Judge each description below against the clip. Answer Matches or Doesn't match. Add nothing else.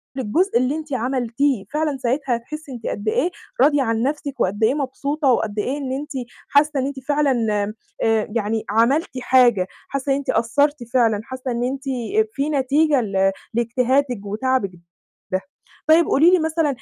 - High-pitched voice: Matches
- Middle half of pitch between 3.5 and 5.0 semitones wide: Matches